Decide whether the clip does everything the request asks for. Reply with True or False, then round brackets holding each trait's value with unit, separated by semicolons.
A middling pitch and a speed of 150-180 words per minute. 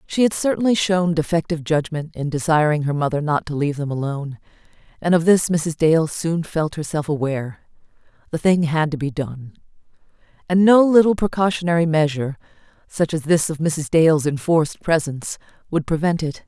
True (160 Hz; 165 wpm)